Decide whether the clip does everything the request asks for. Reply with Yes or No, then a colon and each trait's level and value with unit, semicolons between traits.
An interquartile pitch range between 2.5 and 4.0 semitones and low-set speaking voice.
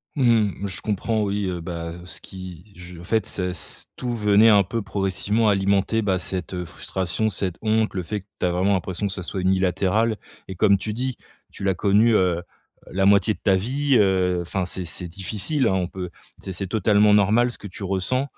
Yes: average, 2.8 semitones; very low, 95 Hz